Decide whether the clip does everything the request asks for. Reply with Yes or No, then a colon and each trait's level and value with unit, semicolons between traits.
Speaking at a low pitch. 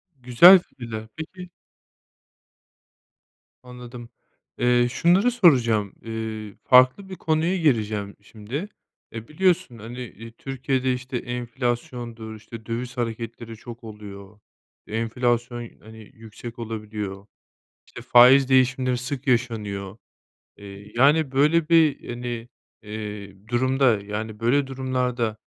Yes: low, 120 Hz